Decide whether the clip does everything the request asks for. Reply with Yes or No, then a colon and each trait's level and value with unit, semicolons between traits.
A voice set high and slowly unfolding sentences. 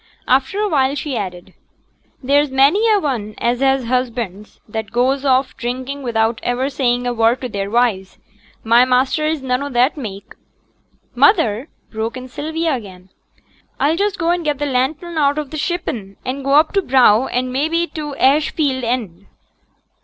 No: very high, 260 Hz; average, 175 wpm